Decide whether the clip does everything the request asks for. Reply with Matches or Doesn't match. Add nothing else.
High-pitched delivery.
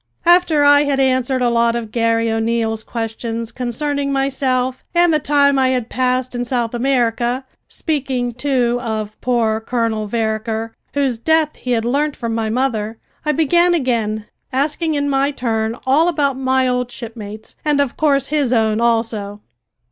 Matches